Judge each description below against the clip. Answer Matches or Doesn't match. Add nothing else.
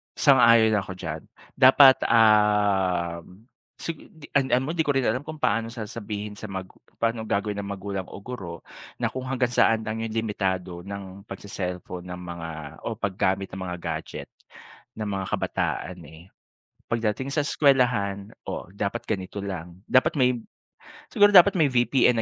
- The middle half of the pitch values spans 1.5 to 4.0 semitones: Doesn't match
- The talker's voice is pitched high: Doesn't match